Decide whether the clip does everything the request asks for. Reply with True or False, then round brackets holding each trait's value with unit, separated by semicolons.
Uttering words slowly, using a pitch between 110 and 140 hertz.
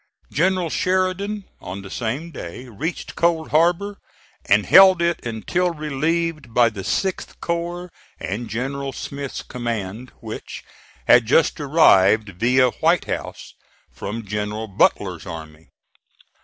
True (120 wpm; 135 Hz)